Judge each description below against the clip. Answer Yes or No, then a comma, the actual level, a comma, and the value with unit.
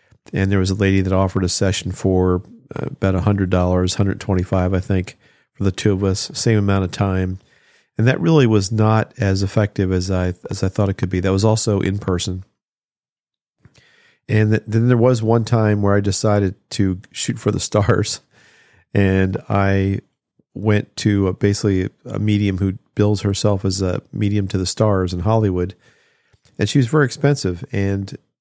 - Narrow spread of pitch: Yes, narrow, 2.3 semitones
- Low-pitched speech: Yes, low, 100 Hz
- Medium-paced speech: Yes, average, 180 wpm